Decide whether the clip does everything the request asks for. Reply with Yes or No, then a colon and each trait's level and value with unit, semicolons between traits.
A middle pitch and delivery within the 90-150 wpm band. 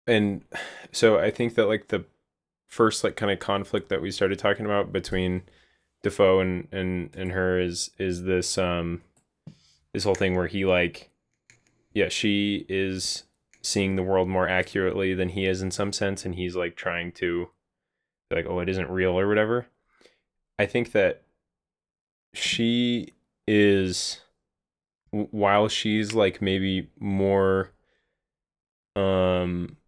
No: very low, 95 Hz; average, 140 wpm